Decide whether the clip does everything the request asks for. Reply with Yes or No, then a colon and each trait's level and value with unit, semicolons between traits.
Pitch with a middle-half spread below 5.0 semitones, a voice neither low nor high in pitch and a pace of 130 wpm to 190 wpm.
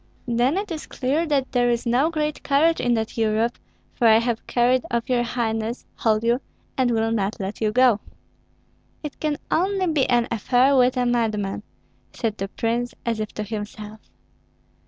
No: average, 2.9 semitones; high, 240 Hz; average, 180 wpm